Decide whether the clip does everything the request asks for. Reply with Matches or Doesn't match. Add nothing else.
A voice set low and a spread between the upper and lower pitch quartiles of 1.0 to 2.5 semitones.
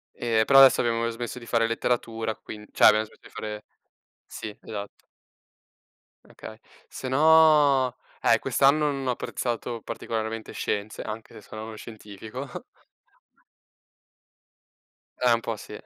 Doesn't match